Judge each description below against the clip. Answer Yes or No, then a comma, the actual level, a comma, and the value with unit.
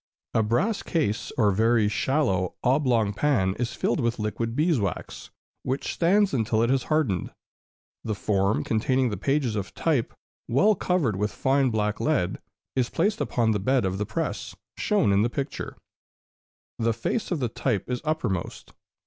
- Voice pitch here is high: No, low, 120 Hz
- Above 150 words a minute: Yes, average, 160 wpm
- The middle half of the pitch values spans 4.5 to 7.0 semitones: Yes, average, 5.1 semitones